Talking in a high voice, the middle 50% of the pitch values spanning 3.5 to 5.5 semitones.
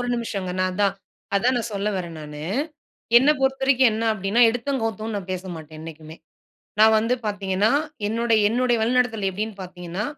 Yes: high, 210 Hz; average, 4.1 semitones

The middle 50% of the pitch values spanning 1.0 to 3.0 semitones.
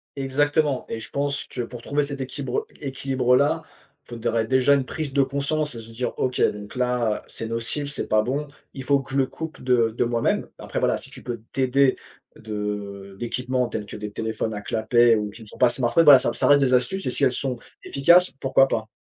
No: average, 3.4 semitones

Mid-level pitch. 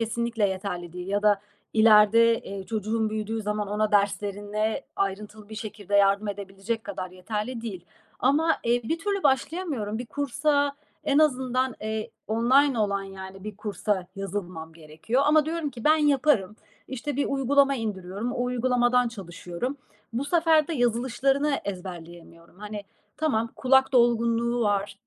No: high, 220 Hz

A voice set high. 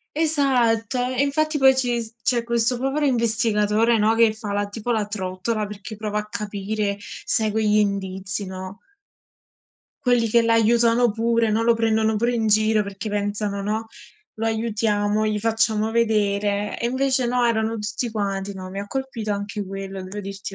Yes: high, 220 Hz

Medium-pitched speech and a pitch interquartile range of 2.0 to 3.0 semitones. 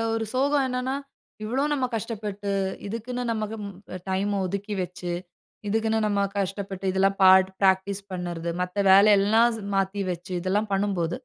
No: high, 200 Hz; average, 2.7 semitones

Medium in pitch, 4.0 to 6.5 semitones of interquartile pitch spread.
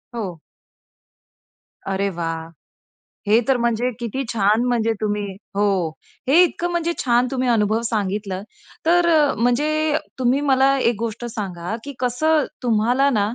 No: high, 235 Hz; average, 4.4 semitones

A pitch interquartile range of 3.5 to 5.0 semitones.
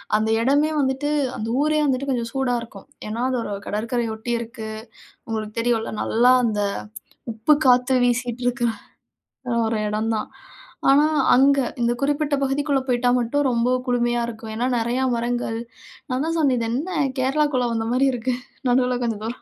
No: average, 2.7 semitones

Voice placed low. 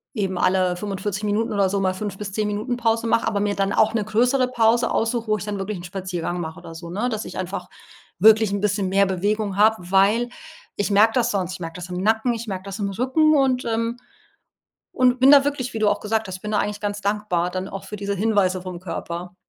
No: high, 205 Hz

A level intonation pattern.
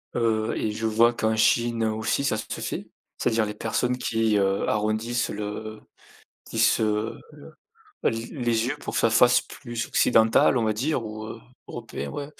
Yes: narrow, 1.6 semitones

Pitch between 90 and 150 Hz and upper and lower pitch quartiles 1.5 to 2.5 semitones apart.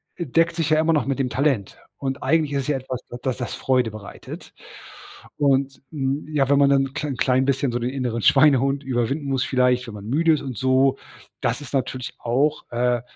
Yes: low, 135 Hz; narrow, 2.1 semitones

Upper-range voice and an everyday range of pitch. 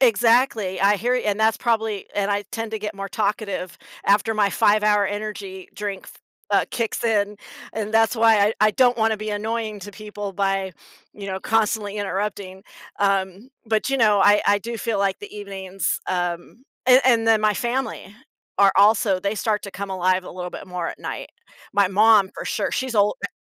No: high, 205 Hz; narrow, 2.0 semitones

